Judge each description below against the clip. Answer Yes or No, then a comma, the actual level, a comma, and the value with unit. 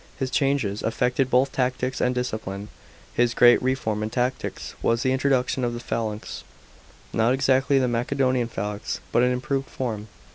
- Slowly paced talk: No, average, 155 wpm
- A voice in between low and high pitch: No, low, 125 Hz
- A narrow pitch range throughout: Yes, narrow, 2.2 semitones